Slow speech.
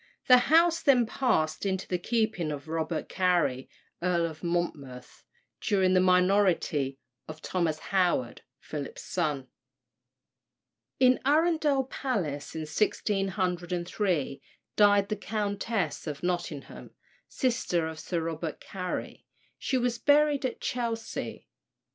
Yes: slow, 110 wpm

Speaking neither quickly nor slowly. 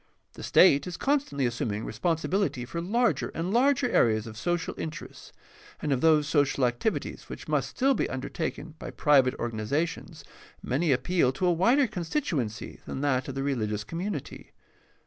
Yes: average, 160 wpm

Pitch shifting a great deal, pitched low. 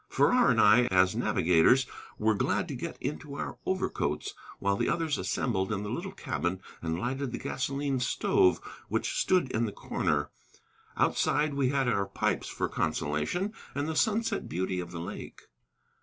Yes: wide, 7.0 semitones; low, 120 Hz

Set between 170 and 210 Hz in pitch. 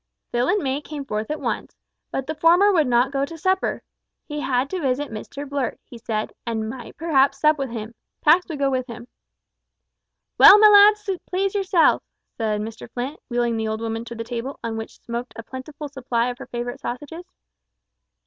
No: very high, 265 Hz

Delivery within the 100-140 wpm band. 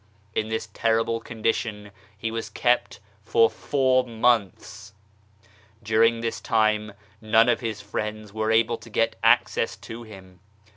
Yes: slow, 135 wpm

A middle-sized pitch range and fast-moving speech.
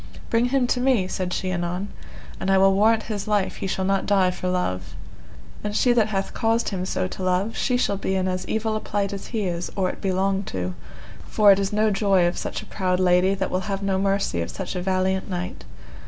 No: narrow, 2.1 semitones; fast, 235 wpm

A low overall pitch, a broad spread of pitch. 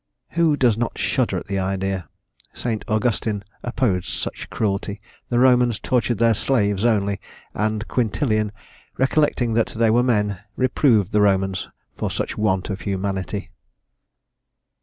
No: low, 110 Hz; average, 3.4 semitones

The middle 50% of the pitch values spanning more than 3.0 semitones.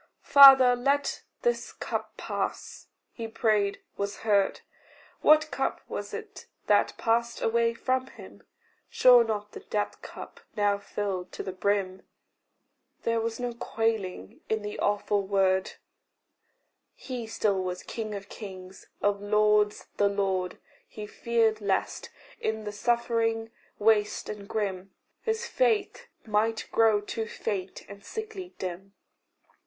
No: average, 2.7 semitones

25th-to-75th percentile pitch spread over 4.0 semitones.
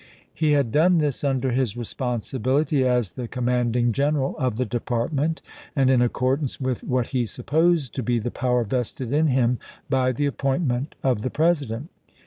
No: average, 2.7 semitones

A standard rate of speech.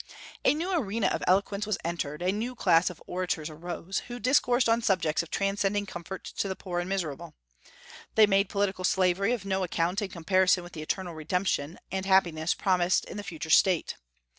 Yes: average, 190 wpm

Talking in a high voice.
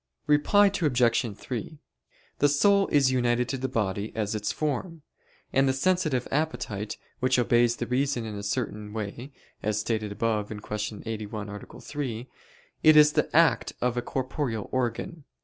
No: low, 120 Hz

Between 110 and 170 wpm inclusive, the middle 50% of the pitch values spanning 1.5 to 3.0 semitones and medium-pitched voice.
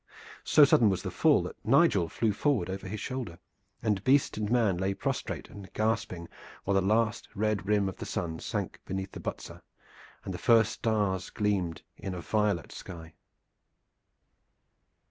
No: average, 160 wpm; average, 2.7 semitones; low, 100 Hz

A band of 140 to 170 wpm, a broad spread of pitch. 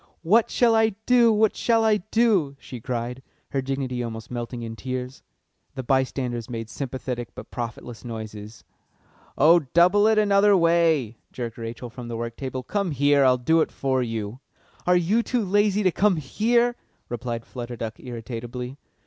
Yes: average, 165 wpm; wide, 8.5 semitones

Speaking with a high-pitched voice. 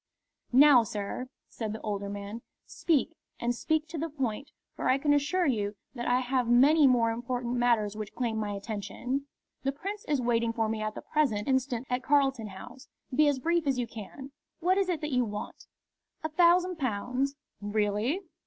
Yes: very high, 250 Hz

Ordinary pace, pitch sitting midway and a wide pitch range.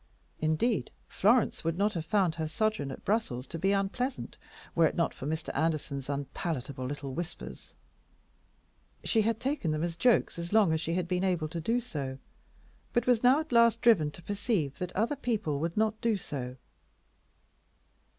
Yes: average, 175 wpm; medium, 175 Hz; wide, 6.1 semitones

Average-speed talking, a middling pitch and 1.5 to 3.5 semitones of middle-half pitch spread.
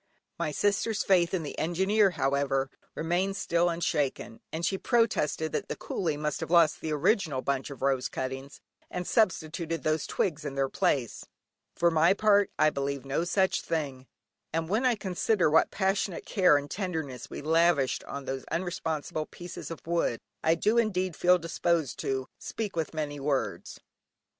No: average, 165 wpm; medium, 165 Hz; average, 4.5 semitones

